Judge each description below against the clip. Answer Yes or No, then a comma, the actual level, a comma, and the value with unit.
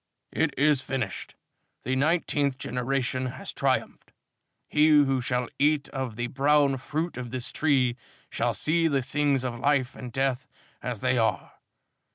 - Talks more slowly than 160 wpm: Yes, average, 150 wpm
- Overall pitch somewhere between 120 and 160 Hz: Yes, low, 135 Hz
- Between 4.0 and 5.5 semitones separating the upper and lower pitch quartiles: No, narrow, 2.6 semitones